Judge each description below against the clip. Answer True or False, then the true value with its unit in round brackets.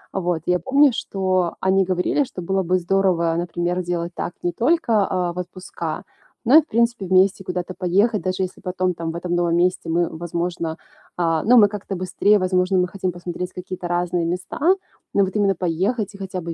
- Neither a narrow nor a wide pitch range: False (1.8 semitones)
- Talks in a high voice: False (180 Hz)